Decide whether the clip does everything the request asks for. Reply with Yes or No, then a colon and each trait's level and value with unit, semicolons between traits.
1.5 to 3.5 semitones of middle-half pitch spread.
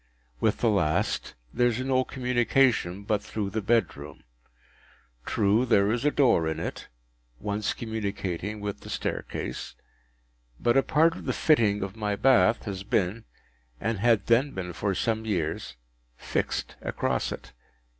No: average, 4.1 semitones